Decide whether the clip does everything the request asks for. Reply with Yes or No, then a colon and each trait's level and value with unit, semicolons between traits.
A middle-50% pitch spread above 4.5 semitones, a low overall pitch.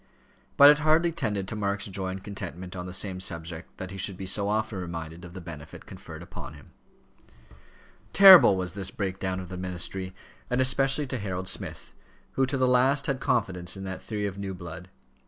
Yes: average, 5.3 semitones; very low, 95 Hz